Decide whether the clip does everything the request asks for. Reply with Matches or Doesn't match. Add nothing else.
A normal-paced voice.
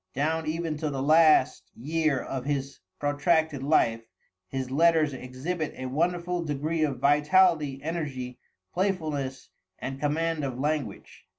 Doesn't match